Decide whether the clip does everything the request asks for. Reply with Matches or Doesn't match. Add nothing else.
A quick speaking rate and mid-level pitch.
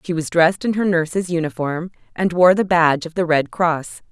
Matches